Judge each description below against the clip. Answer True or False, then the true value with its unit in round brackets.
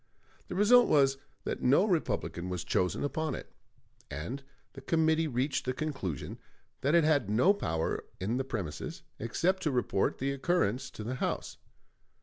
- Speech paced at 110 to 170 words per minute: True (155 wpm)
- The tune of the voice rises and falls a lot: True (6.5 semitones)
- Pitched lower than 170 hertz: True (135 Hz)